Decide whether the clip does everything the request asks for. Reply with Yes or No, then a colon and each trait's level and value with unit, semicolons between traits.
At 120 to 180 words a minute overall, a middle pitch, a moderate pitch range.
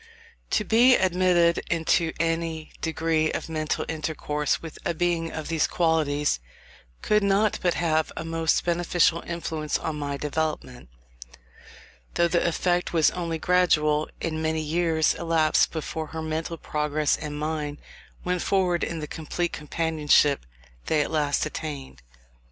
No: average, 140 wpm; medium, 160 Hz; narrow, 1.9 semitones